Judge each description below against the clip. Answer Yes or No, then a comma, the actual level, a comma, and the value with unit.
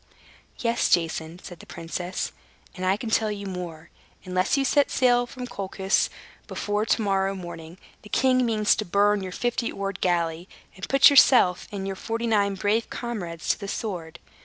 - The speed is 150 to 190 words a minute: Yes, average, 175 wpm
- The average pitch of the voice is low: No, high, 200 Hz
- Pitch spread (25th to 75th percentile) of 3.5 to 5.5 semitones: Yes, average, 4.1 semitones